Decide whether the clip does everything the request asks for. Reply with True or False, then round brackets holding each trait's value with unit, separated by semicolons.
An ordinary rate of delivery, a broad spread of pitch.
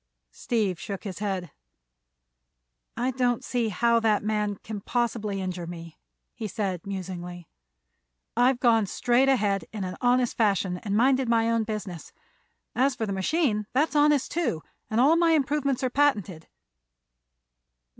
False (145 wpm; 4.6 semitones)